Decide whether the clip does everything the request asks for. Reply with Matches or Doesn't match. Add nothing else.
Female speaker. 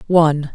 Matches